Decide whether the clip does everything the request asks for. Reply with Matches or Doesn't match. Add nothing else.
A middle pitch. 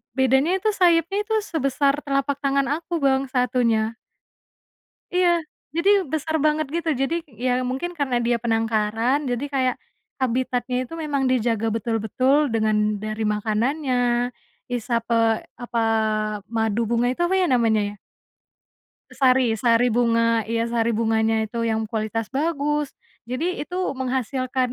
Doesn't match